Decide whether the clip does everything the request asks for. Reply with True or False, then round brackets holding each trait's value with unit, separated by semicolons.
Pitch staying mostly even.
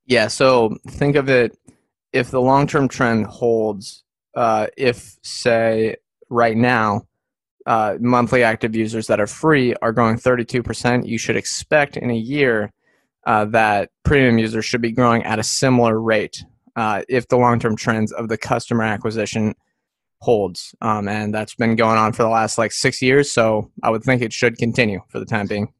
True (2.1 semitones)